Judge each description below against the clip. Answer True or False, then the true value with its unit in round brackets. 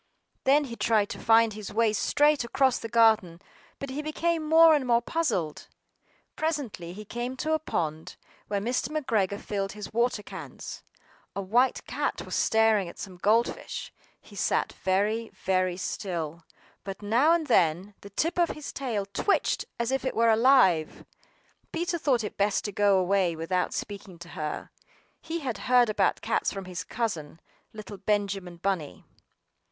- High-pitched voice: True (215 Hz)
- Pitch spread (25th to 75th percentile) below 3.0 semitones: False (5.3 semitones)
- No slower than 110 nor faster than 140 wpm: False (165 wpm)